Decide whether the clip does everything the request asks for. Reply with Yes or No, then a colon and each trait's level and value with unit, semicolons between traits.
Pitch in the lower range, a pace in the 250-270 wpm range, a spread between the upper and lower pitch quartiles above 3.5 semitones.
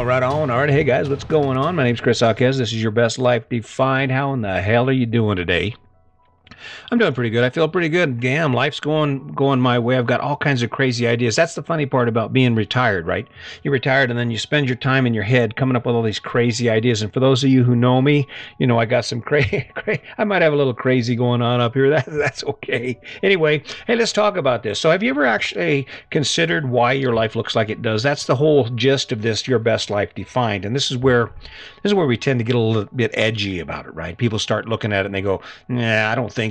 No: low, 125 Hz; fast, 265 wpm; average, 3.2 semitones